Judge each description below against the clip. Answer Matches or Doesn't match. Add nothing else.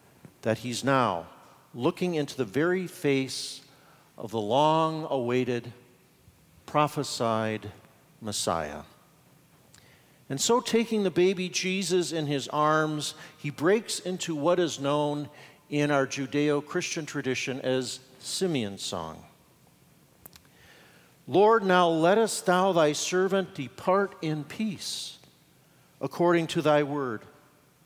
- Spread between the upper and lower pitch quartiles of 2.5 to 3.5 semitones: Doesn't match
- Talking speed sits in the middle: Doesn't match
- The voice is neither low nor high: Matches